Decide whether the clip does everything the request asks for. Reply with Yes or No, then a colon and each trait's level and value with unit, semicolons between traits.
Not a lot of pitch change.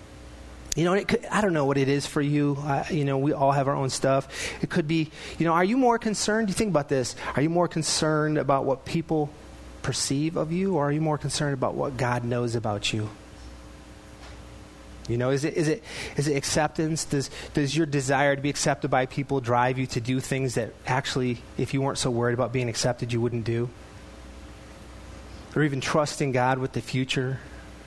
No: average, 3.9 semitones